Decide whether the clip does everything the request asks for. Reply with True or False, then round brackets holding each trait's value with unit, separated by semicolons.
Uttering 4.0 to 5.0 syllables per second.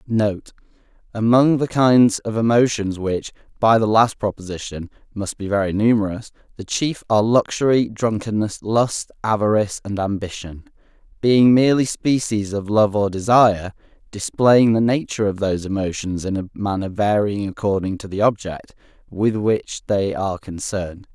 True (4.9 syllables/s)